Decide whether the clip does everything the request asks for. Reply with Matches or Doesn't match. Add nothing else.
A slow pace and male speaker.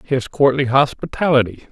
Matches